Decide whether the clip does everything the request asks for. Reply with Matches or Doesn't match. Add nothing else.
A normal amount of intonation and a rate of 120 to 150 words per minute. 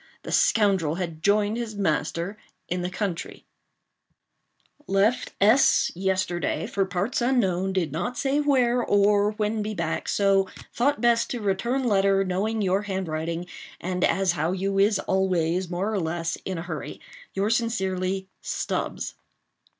Matches